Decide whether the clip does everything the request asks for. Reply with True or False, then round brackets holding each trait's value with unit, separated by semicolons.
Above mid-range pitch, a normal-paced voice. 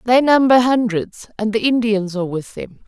True (225 Hz; 190 wpm)